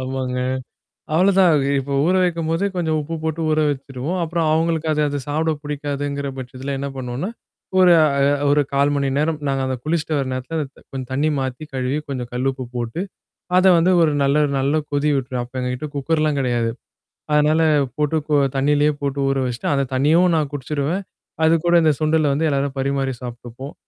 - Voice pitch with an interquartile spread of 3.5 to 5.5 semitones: No, average, 3.0 semitones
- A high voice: No, medium, 145 Hz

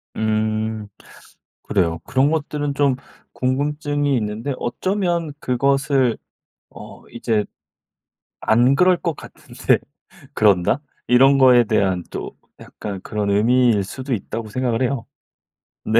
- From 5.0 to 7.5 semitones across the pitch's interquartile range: No, average, 4.5 semitones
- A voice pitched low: Yes, low, 125 Hz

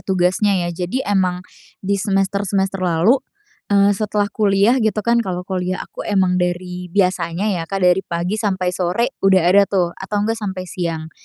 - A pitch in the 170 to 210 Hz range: Yes, high, 190 Hz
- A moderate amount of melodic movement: No, narrow, 2.1 semitones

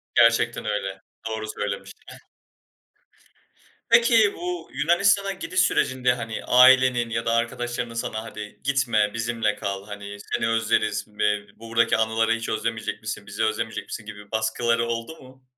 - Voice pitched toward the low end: Yes, low, 115 Hz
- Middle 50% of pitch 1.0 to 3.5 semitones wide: Yes, average, 2.8 semitones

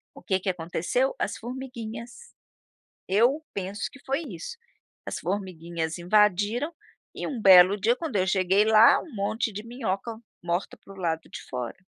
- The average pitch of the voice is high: Yes, high, 205 Hz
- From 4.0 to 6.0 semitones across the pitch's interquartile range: Yes, average, 4.5 semitones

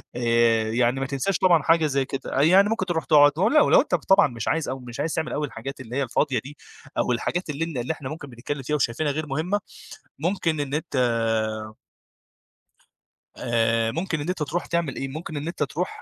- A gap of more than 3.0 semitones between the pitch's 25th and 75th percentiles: Yes, average, 4.0 semitones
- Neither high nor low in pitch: Yes, medium, 145 Hz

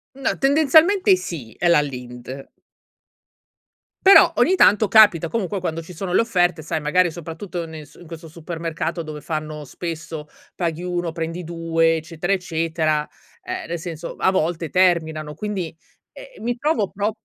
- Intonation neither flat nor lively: Yes, average, 3.1 semitones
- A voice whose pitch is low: No, medium, 170 Hz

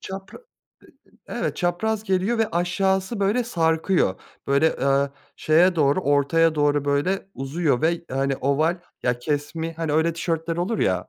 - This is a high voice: No, medium, 165 Hz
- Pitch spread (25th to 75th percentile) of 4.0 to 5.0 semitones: Yes, average, 4.6 semitones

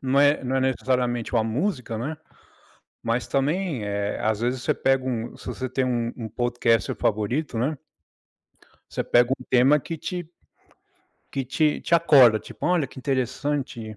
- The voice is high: No, low, 130 Hz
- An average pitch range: Yes, average, 3.4 semitones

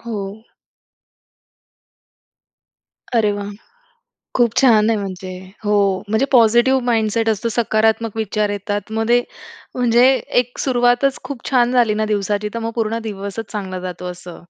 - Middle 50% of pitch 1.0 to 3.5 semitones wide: Yes, narrow, 2.6 semitones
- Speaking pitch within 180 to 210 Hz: No, high, 220 Hz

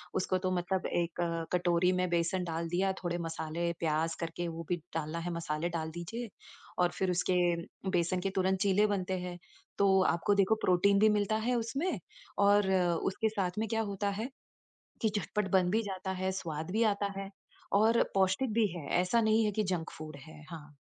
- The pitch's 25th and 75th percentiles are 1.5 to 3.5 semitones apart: Yes, average, 3.0 semitones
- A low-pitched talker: No, medium, 185 Hz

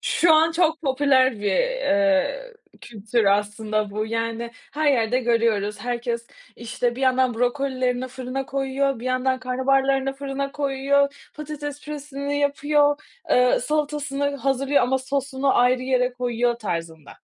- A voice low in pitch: No, very high, 260 Hz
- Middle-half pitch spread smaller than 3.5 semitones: Yes, average, 3.0 semitones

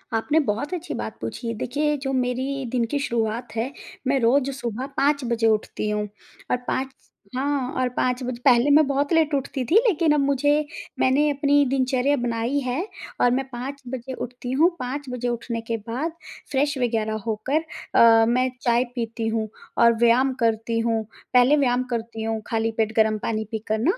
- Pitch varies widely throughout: No, average, 3.3 semitones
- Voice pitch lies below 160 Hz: No, very high, 250 Hz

